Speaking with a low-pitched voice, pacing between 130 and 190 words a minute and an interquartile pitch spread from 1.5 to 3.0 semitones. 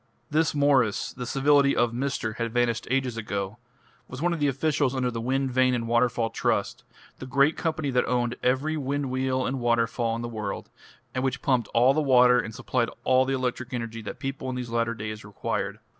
No: low, 125 Hz; fast, 205 wpm; narrow, 2.5 semitones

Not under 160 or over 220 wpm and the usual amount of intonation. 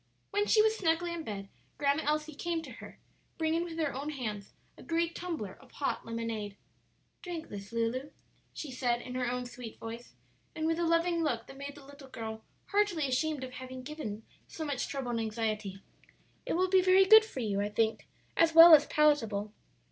No: average, 195 wpm; wide, 6.2 semitones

